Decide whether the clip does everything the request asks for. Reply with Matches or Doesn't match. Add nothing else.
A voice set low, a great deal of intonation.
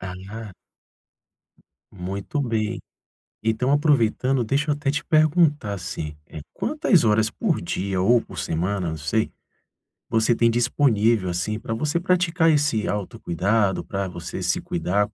Matches